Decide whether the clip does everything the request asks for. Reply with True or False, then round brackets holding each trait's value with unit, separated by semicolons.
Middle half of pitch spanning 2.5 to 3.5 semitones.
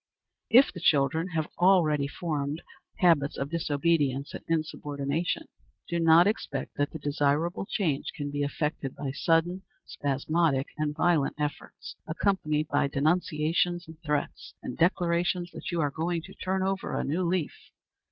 True (3.2 semitones)